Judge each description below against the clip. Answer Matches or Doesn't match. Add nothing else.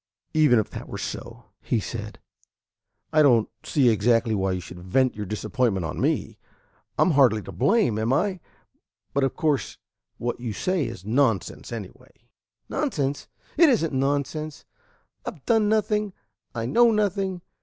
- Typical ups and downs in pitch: Doesn't match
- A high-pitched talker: Doesn't match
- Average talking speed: Matches